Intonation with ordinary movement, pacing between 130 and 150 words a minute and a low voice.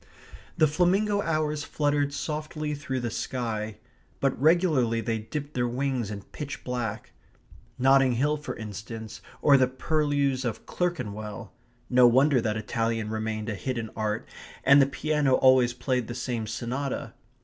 Yes: average, 4.3 semitones; average, 145 wpm; low, 130 Hz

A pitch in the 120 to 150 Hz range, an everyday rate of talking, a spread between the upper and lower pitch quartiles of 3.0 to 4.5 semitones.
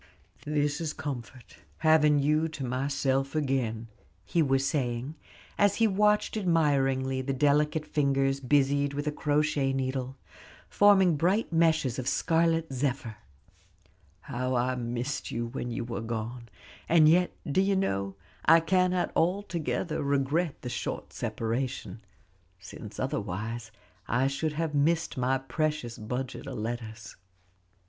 No: medium, 140 Hz; slow, 130 wpm; average, 4.1 semitones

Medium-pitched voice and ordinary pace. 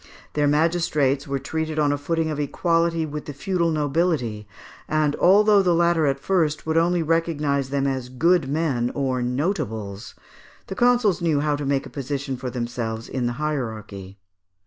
Yes: medium, 150 Hz; average, 170 wpm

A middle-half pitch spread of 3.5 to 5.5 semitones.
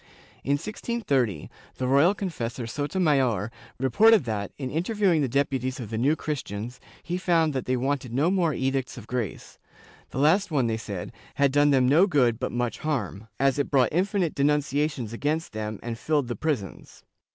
Yes: average, 4.5 semitones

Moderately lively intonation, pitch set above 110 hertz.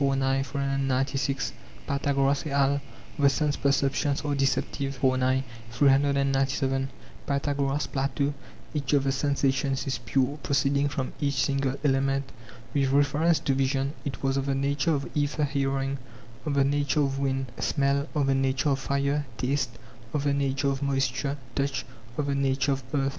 No: narrow, 0.9 semitones; medium, 140 Hz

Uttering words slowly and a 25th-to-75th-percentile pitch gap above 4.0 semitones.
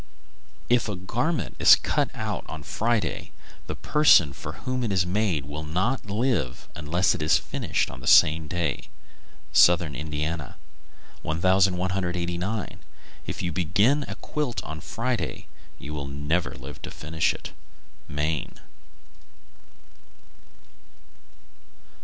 Yes: slow, 120 wpm; average, 5.3 semitones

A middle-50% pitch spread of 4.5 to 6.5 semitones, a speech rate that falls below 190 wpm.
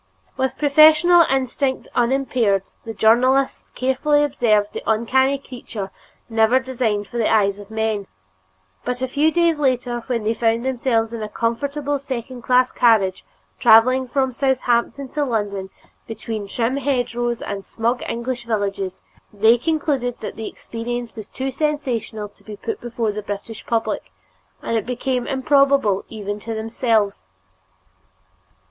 No: average, 3.1 semitones; average, 140 wpm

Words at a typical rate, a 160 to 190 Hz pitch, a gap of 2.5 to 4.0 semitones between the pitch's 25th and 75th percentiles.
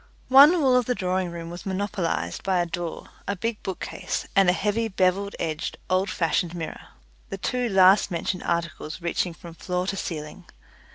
Yes: average, 175 wpm; medium, 185 Hz; average, 2.8 semitones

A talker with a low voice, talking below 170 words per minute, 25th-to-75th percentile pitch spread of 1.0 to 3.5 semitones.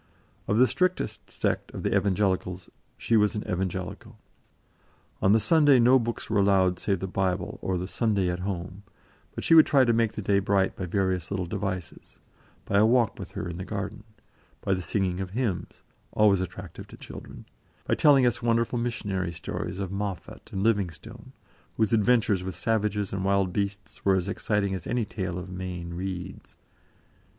No: low, 100 Hz; average, 180 wpm; average, 3.1 semitones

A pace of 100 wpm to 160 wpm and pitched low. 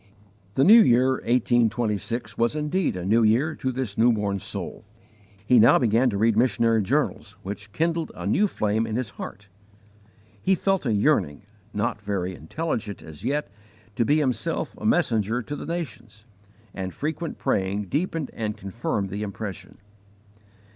Yes: average, 155 wpm; low, 115 Hz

